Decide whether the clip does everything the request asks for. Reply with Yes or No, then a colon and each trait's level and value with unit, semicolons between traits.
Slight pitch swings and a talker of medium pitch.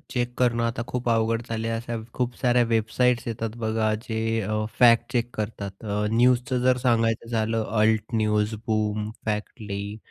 No: narrow, 1.8 semitones; low, 115 Hz